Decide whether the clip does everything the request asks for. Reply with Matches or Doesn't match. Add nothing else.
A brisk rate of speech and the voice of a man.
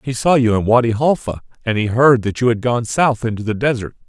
Matches